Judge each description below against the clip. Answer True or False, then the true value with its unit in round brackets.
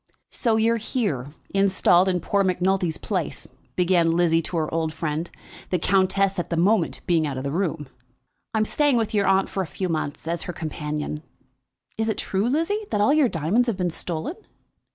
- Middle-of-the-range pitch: True (180 Hz)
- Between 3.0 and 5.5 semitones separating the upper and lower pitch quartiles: True (4.1 semitones)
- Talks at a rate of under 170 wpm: False (195 wpm)